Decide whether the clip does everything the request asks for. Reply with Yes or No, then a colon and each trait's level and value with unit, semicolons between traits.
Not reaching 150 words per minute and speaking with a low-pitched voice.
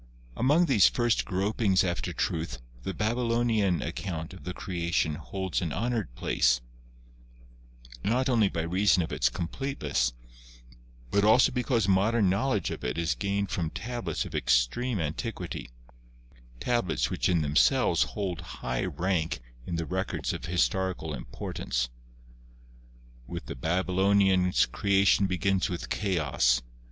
Yes: slow, 135 wpm; very low, 95 Hz